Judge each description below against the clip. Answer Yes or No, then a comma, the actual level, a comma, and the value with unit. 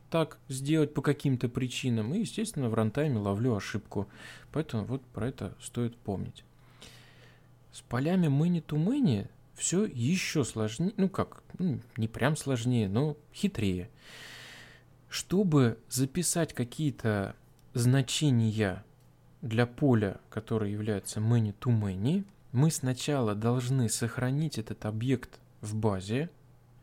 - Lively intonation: No, average, 4.8 semitones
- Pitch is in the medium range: No, low, 125 Hz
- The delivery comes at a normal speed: No, slow, 105 wpm